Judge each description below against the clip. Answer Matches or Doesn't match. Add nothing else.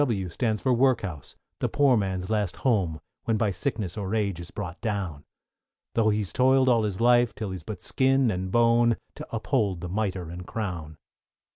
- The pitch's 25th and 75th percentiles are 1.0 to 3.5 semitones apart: Doesn't match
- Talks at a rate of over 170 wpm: Matches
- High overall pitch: Doesn't match